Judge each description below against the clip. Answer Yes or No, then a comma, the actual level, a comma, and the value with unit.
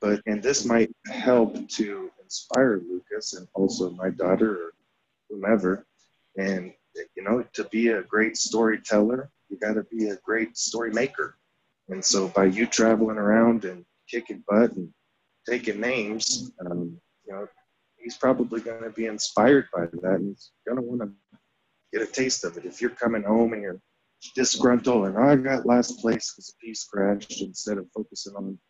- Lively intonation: No, average, 3.1 semitones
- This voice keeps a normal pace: Yes, average, 170 wpm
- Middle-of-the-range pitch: No, low, 110 Hz